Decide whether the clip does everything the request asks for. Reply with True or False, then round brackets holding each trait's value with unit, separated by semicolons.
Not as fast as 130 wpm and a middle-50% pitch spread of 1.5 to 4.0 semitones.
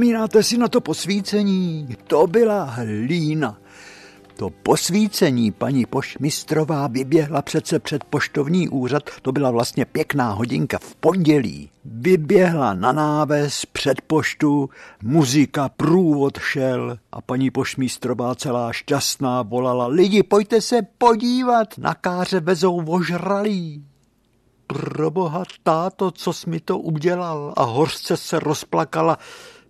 False (115 wpm; 6.0 semitones)